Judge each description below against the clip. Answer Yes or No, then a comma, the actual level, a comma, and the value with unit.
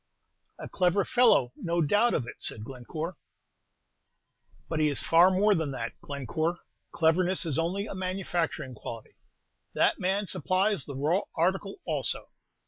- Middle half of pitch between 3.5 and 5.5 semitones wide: Yes, average, 4.5 semitones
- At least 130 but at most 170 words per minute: Yes, average, 140 wpm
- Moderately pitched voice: Yes, medium, 170 Hz